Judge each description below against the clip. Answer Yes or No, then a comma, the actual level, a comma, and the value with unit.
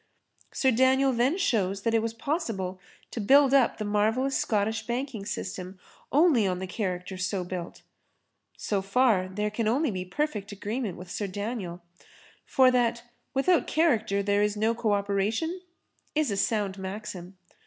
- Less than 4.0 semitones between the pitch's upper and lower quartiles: No, average, 4.6 semitones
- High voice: Yes, high, 215 Hz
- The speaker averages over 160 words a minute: No, average, 155 wpm